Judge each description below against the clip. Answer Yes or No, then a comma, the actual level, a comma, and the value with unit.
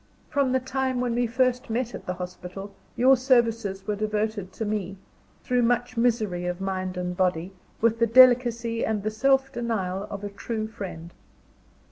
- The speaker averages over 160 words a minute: Yes, average, 170 wpm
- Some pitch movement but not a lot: Yes, average, 4.1 semitones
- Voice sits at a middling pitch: No, high, 220 Hz